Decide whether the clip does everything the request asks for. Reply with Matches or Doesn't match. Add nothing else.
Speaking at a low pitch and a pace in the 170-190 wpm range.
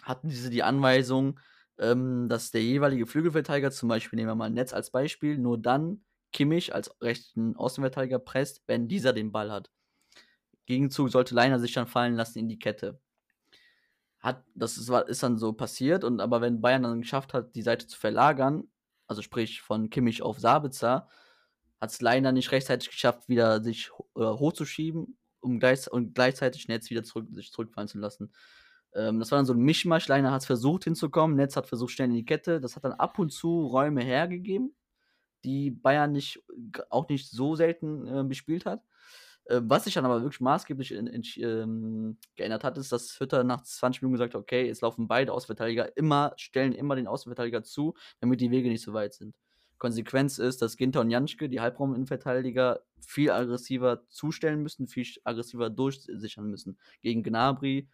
Matches